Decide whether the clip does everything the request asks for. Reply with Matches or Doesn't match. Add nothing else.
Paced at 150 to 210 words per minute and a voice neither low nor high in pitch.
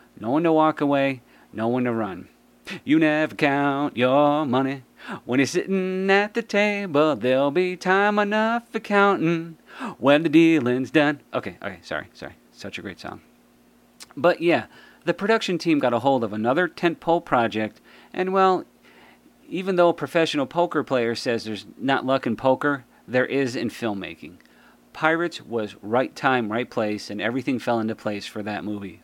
Matches